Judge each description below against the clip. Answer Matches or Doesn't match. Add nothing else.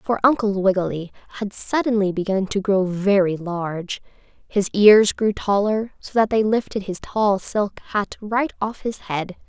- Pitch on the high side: Matches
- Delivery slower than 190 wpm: Matches